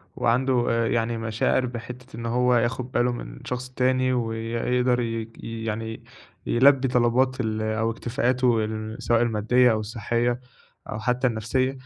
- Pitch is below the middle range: Yes, low, 120 Hz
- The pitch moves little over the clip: Yes, narrow, 1.9 semitones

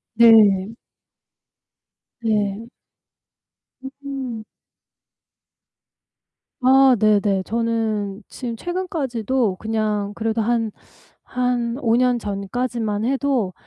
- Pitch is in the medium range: No, high, 225 Hz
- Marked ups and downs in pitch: No, average, 3.0 semitones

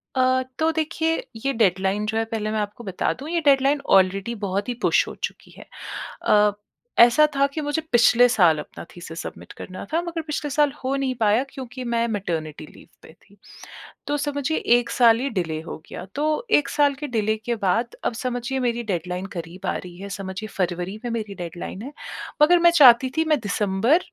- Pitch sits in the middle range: No, high, 235 Hz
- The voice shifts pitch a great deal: Yes, wide, 6.1 semitones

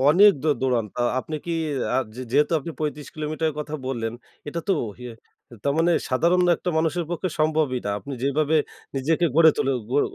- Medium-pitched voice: Yes, medium, 155 Hz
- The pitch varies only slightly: No, average, 3.3 semitones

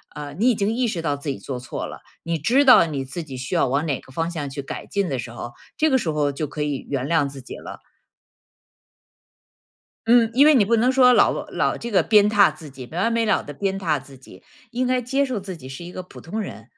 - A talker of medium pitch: Yes, medium, 170 Hz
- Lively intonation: Yes, wide, 8.3 semitones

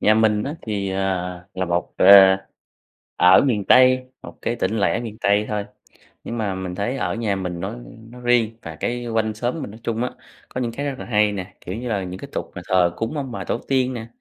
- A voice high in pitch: No, low, 110 Hz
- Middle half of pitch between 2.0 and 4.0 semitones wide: Yes, average, 3.6 semitones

